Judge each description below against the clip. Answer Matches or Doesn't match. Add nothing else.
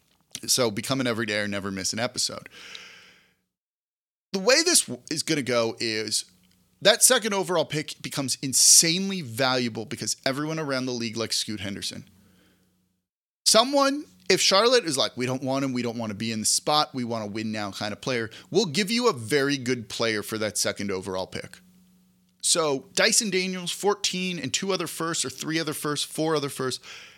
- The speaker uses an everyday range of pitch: Doesn't match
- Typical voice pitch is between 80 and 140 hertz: Matches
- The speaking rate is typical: Matches